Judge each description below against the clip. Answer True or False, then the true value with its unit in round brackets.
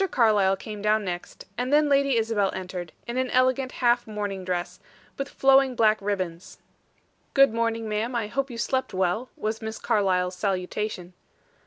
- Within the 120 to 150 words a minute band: False (160 wpm)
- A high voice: True (215 Hz)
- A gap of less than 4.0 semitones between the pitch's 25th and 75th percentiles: False (4.6 semitones)